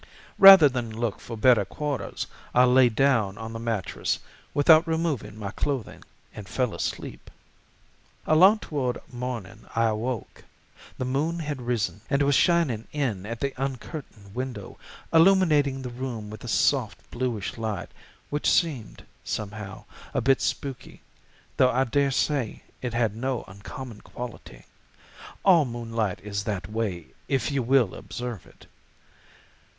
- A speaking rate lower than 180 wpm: Yes, average, 140 wpm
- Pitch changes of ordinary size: Yes, average, 4.2 semitones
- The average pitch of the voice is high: No, low, 125 Hz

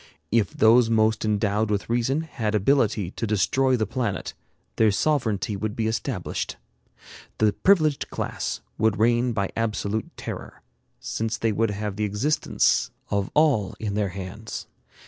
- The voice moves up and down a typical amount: No, narrow, 2.3 semitones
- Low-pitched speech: Yes, low, 110 Hz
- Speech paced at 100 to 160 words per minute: Yes, average, 145 wpm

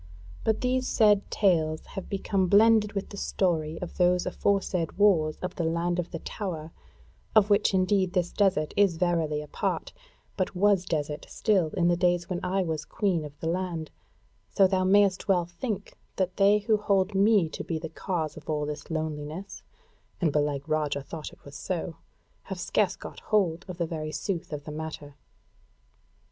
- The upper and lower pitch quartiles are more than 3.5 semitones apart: Yes, average, 3.9 semitones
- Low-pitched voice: No, medium, 175 Hz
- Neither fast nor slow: Yes, average, 180 wpm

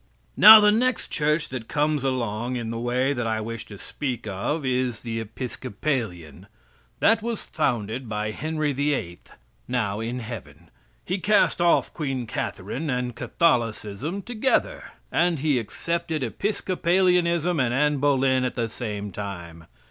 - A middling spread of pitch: No, wide, 6.1 semitones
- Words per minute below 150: Yes, average, 140 wpm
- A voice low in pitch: Yes, low, 130 Hz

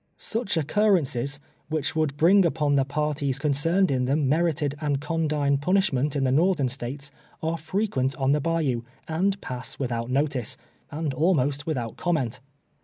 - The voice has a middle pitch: Yes, medium, 145 Hz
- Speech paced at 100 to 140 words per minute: No, average, 155 wpm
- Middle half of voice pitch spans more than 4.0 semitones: No, average, 3.4 semitones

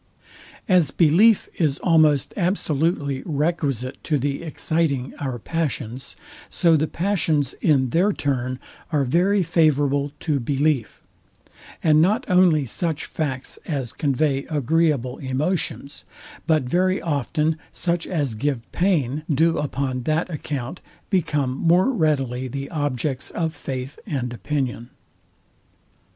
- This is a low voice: No, medium, 150 Hz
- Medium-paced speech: No, slow, 115 wpm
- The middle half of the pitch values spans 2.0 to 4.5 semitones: Yes, average, 3.7 semitones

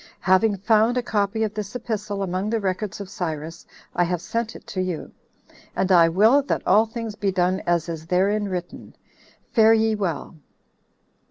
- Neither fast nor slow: Yes, average, 170 wpm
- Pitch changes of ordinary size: Yes, average, 3.4 semitones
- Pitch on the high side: Yes, high, 200 Hz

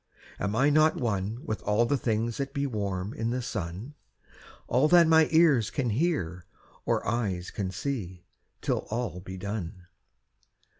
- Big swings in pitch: Yes, wide, 6.7 semitones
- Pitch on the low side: Yes, low, 115 Hz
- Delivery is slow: No, average, 155 wpm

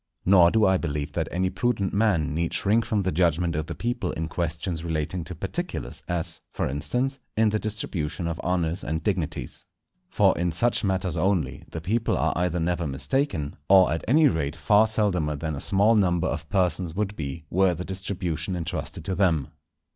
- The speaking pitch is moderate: No, very low, 90 Hz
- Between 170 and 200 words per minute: Yes, average, 185 wpm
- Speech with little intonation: No, average, 3.9 semitones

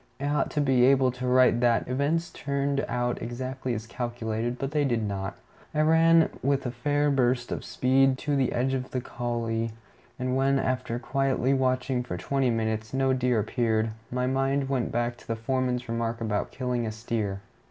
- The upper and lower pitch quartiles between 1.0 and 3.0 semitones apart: Yes, narrow, 2.4 semitones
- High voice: No, low, 125 Hz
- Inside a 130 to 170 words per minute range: No, average, 185 wpm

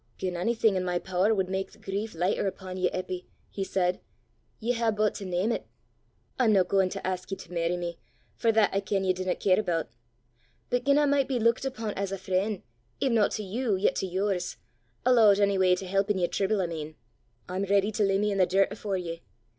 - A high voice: Yes, high, 195 Hz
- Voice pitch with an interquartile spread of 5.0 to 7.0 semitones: No, average, 2.7 semitones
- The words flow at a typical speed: No, fast, 225 wpm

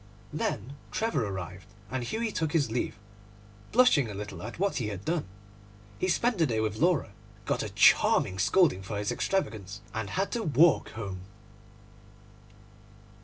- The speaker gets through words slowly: No, average, 155 wpm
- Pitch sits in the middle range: No, low, 120 Hz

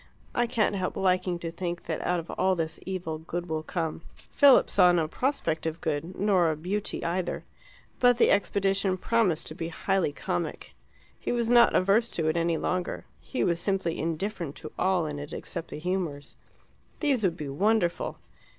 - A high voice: No, medium, 180 Hz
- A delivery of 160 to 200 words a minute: Yes, average, 180 wpm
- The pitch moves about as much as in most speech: Yes, average, 3.3 semitones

